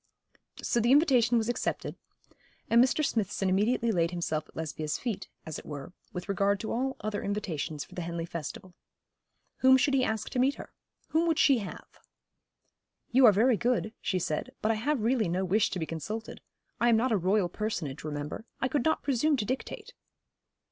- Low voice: No, high, 215 Hz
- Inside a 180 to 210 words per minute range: Yes, average, 190 wpm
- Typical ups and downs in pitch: No, wide, 6.1 semitones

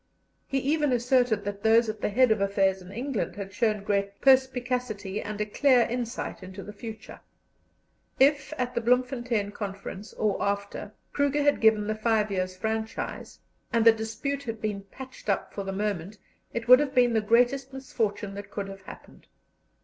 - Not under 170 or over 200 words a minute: Yes, average, 175 wpm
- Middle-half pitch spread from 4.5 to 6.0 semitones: No, average, 3.7 semitones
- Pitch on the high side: Yes, high, 220 Hz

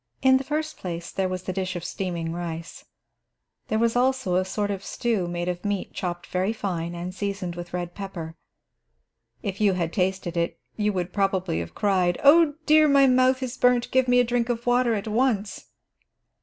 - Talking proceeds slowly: No, average, 195 wpm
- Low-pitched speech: No, high, 195 Hz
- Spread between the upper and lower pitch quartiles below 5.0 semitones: No, wide, 5.6 semitones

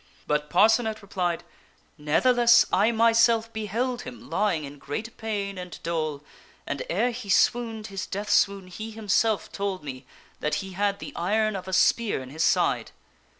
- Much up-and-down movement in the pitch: No, average, 4.2 semitones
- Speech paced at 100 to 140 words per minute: No, average, 165 wpm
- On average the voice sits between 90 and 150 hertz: No, high, 200 Hz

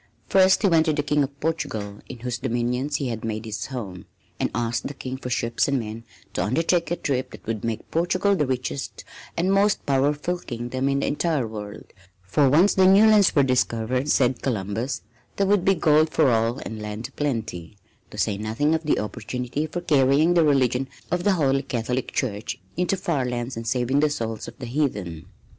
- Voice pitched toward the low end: Yes, low, 130 Hz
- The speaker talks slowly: No, average, 200 wpm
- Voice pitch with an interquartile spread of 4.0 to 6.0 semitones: Yes, average, 5.1 semitones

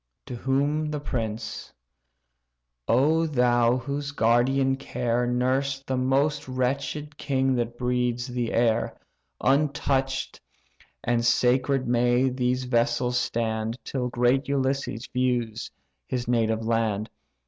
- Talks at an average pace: No, slow, 110 wpm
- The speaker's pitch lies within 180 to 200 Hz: No, low, 125 Hz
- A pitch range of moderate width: No, narrow, 2.0 semitones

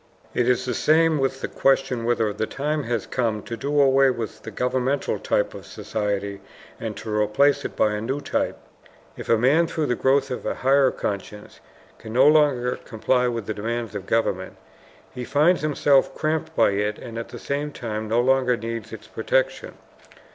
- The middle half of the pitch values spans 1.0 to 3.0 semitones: No, average, 4.0 semitones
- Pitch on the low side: Yes, low, 125 Hz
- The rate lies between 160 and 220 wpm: Yes, average, 190 wpm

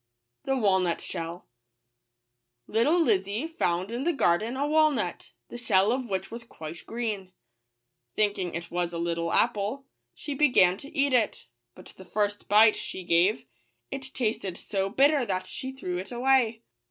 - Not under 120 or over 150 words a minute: No, average, 165 wpm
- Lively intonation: Yes, wide, 6.1 semitones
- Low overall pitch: No, high, 215 Hz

